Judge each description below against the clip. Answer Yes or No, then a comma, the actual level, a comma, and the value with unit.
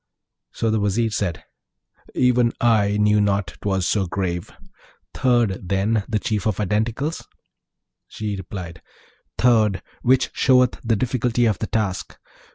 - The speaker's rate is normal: No, slow, 130 wpm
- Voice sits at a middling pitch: No, low, 105 Hz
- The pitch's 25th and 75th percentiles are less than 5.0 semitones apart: Yes, average, 3.1 semitones